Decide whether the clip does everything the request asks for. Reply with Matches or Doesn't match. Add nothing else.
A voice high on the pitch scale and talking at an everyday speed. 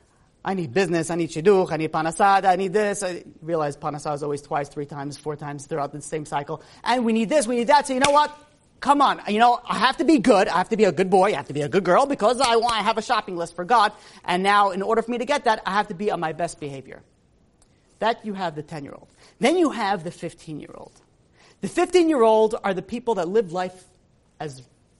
Doesn't match